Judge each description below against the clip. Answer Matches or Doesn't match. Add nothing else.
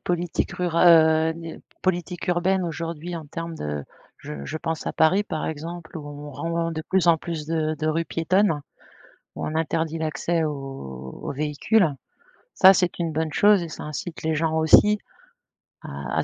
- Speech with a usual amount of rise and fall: Doesn't match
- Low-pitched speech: Doesn't match